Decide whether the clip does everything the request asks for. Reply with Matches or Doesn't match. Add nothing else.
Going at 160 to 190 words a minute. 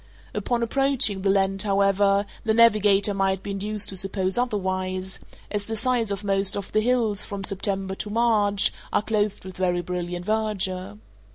Matches